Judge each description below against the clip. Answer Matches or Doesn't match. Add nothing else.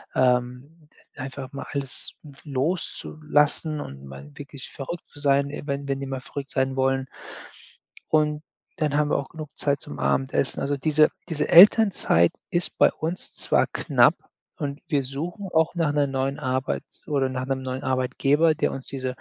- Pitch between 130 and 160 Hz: Matches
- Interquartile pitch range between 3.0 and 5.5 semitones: Doesn't match